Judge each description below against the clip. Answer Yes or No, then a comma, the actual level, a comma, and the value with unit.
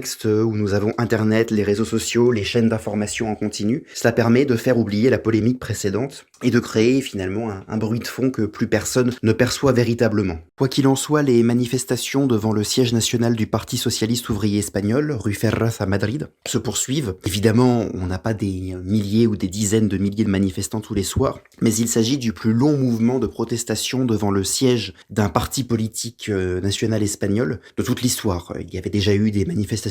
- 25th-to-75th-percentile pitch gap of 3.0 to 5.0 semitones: No, narrow, 2.5 semitones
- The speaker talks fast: No, average, 200 wpm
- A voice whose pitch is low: Yes, low, 110 Hz